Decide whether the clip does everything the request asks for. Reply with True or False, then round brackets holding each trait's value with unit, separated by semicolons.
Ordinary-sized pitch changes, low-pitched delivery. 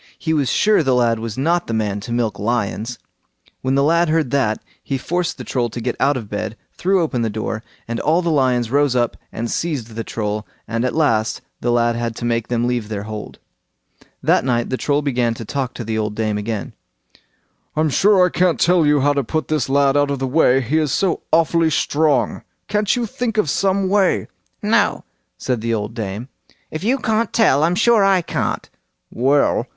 False (5.8 semitones; 130 Hz)